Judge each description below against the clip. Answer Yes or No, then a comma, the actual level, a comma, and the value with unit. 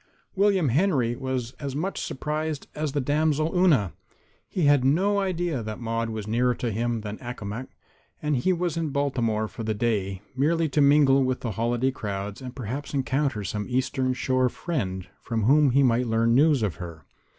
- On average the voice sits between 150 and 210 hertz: No, low, 130 Hz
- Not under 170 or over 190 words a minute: Yes, average, 180 wpm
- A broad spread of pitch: No, average, 4.7 semitones